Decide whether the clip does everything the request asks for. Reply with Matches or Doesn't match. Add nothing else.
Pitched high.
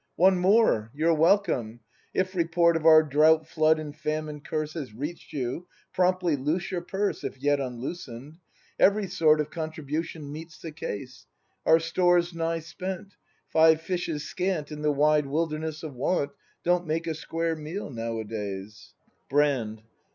Doesn't match